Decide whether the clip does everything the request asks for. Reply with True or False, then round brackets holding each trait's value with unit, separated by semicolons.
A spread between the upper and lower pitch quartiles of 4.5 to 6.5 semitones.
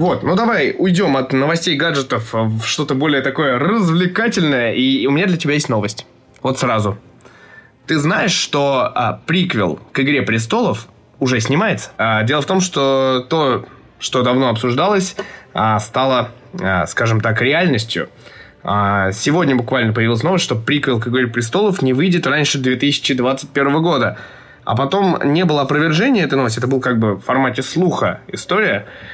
True (5.2 semitones)